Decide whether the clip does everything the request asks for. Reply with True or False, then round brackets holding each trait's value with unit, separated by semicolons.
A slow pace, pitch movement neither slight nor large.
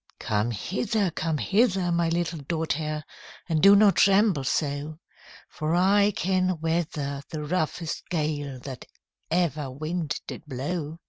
True (130 wpm; 3.5 semitones)